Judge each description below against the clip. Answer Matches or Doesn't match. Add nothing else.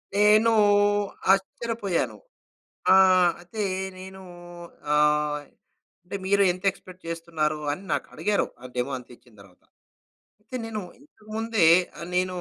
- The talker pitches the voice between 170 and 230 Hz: Matches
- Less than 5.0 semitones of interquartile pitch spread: Doesn't match